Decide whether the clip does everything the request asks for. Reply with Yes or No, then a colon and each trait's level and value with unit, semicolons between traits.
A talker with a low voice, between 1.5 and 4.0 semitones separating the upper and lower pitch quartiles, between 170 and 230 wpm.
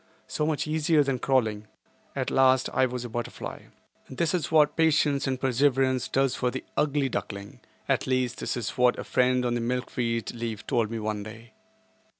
Yes: low, 125 Hz; average, 2.7 semitones; average, 180 wpm